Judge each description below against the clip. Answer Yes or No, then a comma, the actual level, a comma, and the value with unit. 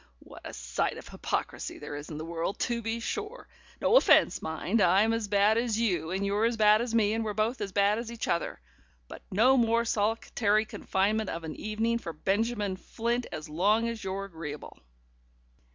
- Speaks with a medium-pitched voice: No, high, 210 Hz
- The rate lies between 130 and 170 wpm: No, average, 195 wpm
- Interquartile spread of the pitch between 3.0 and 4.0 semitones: Yes, average, 3.4 semitones